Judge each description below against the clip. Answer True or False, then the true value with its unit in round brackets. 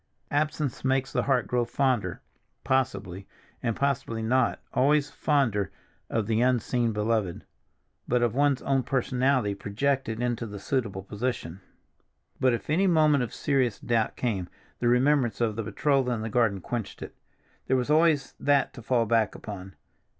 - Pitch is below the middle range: True (125 Hz)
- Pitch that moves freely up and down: False (3.6 semitones)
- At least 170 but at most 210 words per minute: False (150 wpm)